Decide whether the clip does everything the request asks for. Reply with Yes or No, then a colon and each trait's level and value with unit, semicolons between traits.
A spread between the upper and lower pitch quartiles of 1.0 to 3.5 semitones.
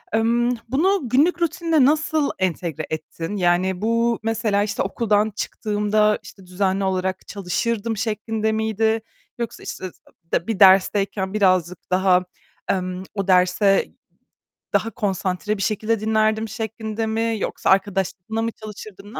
Yes: average, 2.9 semitones